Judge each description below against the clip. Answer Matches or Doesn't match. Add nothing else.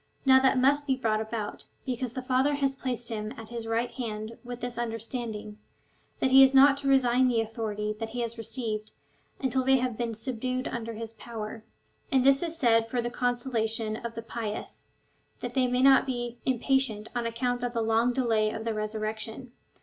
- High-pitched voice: Matches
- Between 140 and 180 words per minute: Doesn't match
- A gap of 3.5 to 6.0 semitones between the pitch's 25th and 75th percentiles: Doesn't match